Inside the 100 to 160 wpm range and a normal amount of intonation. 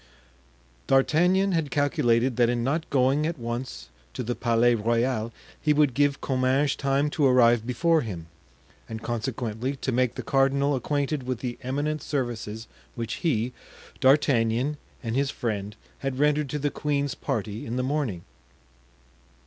Yes: average, 150 wpm; average, 3.5 semitones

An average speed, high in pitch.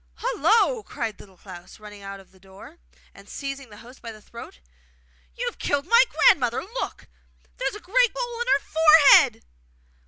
Yes: average, 180 wpm; very high, 275 Hz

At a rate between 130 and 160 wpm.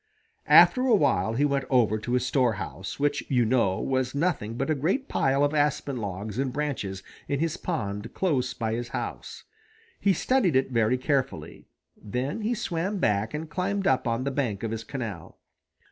No: average, 180 wpm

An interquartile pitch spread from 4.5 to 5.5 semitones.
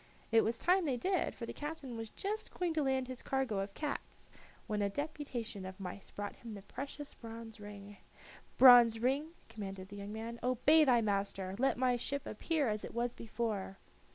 Yes: average, 4.8 semitones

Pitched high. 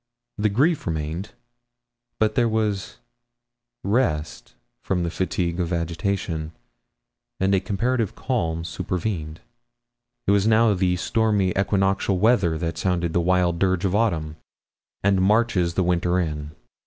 No: very low, 95 Hz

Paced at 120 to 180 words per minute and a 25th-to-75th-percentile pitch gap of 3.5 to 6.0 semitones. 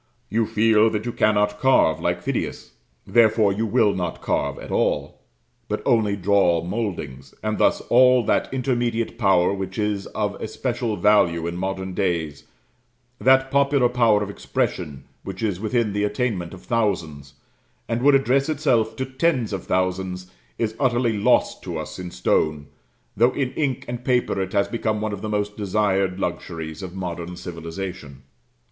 Yes: average, 160 wpm; average, 4.4 semitones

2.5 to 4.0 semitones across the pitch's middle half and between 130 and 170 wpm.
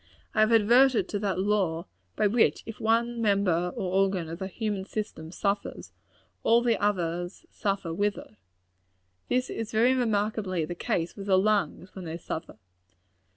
Yes: average, 3.3 semitones; average, 160 wpm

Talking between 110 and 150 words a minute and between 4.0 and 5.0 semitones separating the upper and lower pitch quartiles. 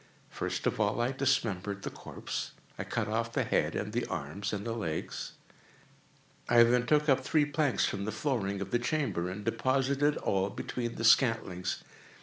No: average, 175 wpm; average, 4.7 semitones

